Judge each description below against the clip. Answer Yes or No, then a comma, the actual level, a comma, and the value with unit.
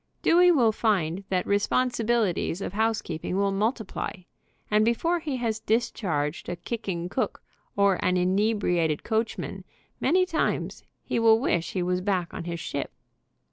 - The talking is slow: No, average, 145 wpm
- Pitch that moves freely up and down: No, average, 4.5 semitones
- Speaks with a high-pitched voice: Yes, high, 205 Hz